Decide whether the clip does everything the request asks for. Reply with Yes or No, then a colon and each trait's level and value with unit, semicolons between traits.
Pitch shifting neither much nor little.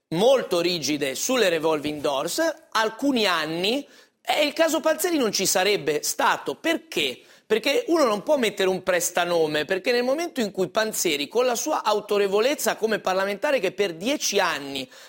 No: wide, 8.2 semitones